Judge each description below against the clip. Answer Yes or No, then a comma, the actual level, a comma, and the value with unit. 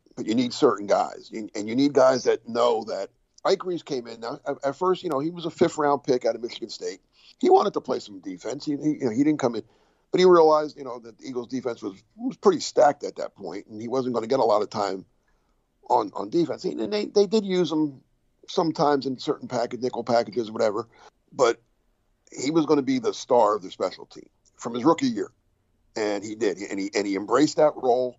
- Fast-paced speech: Yes, fast, 240 wpm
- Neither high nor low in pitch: Yes, medium, 145 Hz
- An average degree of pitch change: No, wide, 6.9 semitones